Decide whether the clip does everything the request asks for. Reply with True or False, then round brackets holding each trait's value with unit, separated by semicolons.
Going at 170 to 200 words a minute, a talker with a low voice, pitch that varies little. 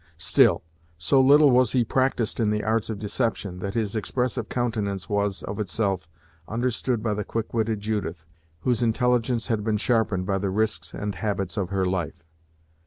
False (175 wpm; 105 Hz; 3.1 semitones)